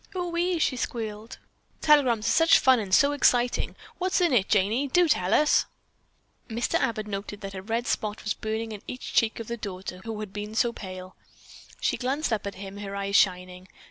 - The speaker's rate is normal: Yes, average, 195 wpm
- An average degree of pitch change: Yes, average, 4.3 semitones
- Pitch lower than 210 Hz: No, high, 220 Hz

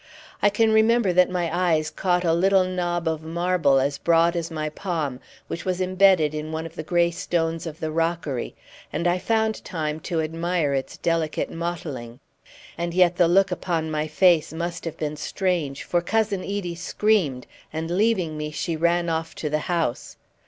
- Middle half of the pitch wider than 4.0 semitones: No, narrow, 2.6 semitones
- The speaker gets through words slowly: No, average, 180 wpm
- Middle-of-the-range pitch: Yes, medium, 170 Hz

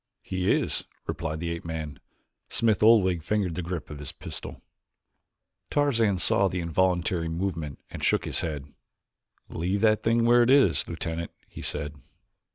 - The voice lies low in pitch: Yes, very low, 90 Hz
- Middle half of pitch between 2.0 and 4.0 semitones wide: No, average, 4.6 semitones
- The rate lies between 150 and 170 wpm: Yes, average, 155 wpm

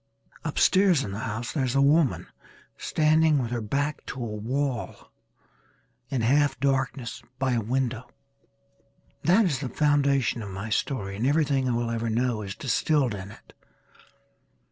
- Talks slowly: No, average, 155 wpm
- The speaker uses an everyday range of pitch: Yes, average, 3.8 semitones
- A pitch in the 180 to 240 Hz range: No, low, 130 Hz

